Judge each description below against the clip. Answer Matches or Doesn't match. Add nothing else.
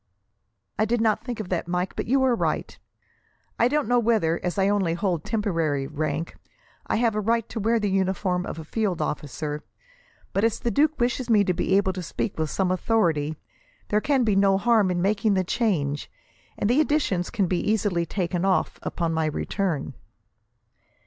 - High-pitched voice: Matches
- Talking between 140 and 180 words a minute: Doesn't match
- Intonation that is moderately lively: Matches